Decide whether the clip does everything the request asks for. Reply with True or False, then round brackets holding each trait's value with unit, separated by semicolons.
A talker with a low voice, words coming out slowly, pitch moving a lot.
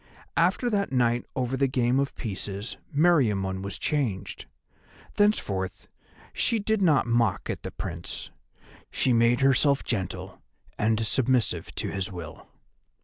True (120 Hz; 130 wpm; 5.7 semitones)